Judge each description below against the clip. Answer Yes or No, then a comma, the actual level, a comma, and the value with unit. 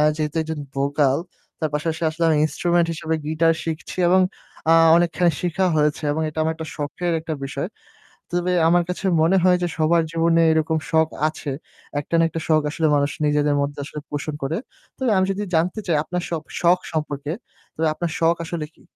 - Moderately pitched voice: Yes, medium, 160 Hz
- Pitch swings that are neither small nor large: No, narrow, 2.1 semitones